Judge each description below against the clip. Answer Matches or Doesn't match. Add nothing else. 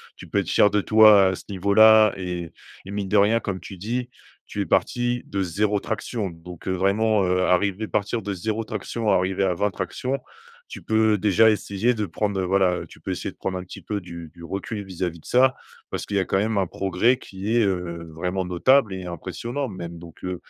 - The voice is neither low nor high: Doesn't match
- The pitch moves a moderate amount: Matches